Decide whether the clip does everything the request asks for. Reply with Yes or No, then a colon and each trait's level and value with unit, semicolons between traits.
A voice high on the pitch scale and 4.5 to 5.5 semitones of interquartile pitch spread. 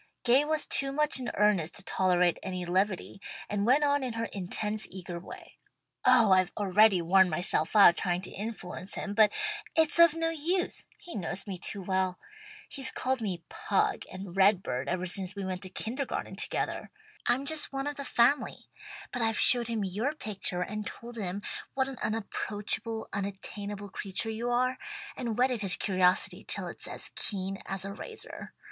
Yes: high, 210 Hz; average, 5.0 semitones